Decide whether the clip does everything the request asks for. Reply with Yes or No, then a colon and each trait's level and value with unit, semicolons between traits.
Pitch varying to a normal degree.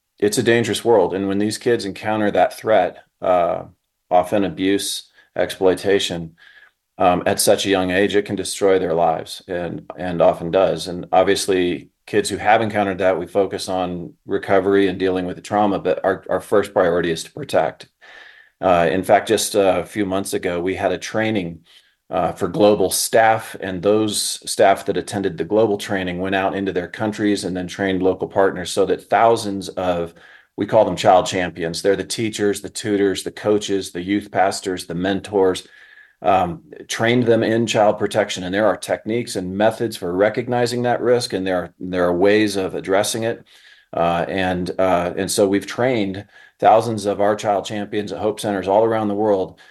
No: narrow, 2.3 semitones